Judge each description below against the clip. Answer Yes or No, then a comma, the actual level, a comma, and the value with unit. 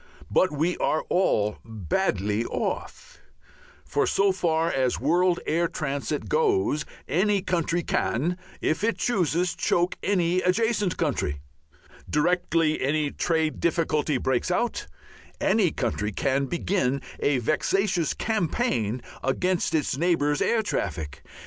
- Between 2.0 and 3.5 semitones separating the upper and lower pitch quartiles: No, average, 4.9 semitones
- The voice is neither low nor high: Yes, medium, 165 Hz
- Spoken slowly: Yes, slow, 115 wpm